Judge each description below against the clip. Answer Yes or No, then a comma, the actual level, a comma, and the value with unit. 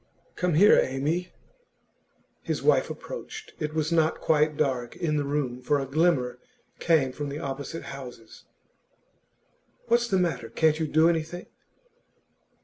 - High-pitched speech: No, medium, 150 Hz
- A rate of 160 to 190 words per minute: No, average, 140 wpm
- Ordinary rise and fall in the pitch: Yes, average, 3.5 semitones